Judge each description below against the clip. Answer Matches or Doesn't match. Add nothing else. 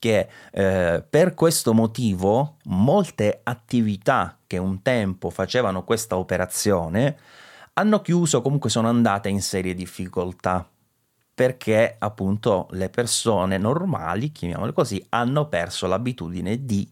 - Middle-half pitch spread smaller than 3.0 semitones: Doesn't match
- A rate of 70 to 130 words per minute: Matches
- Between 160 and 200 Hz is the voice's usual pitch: Doesn't match